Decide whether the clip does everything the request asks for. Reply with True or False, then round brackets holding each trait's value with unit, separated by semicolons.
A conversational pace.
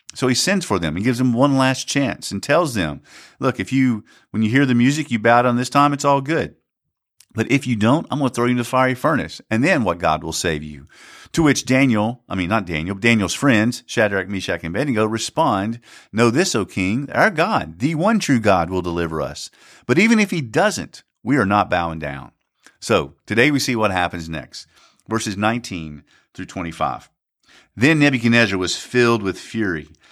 False (210 wpm)